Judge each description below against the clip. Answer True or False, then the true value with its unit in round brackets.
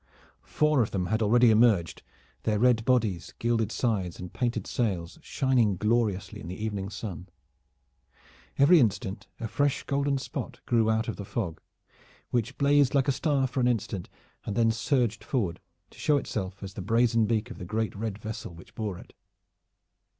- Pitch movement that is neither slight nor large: True (3.7 semitones)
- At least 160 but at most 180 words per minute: True (170 wpm)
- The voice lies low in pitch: True (110 Hz)